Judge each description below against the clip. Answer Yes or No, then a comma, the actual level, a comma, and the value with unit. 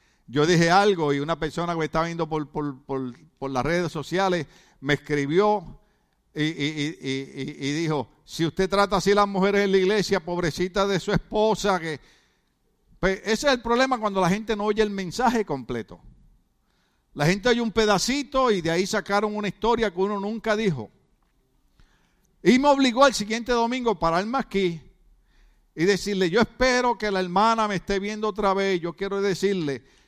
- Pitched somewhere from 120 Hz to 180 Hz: No, high, 190 Hz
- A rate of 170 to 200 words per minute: Yes, average, 185 wpm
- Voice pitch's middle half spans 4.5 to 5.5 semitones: Yes, average, 4.9 semitones